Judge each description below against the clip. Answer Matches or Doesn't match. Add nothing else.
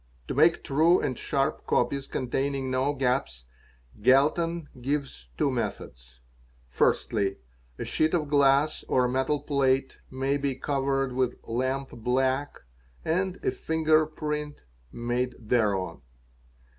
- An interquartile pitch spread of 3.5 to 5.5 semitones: Doesn't match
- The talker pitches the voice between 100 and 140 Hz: Matches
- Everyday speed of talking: Doesn't match